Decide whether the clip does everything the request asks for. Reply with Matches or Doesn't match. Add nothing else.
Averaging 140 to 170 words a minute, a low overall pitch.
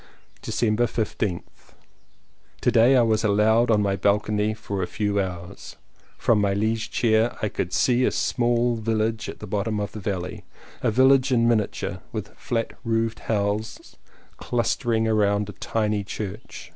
Matches